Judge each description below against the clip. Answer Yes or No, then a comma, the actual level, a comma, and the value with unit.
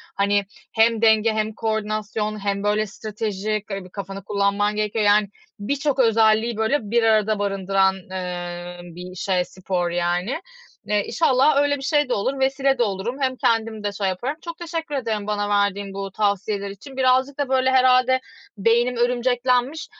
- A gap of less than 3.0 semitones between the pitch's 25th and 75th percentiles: No, average, 4.1 semitones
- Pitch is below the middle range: No, high, 215 Hz